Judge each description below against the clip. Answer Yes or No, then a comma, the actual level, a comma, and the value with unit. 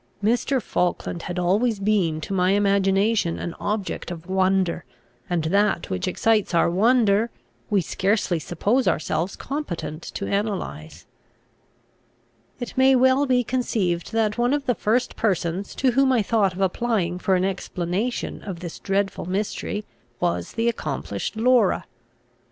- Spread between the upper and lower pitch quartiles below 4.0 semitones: No, average, 4.4 semitones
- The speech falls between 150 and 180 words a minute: No, average, 140 wpm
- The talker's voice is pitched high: Yes, high, 200 Hz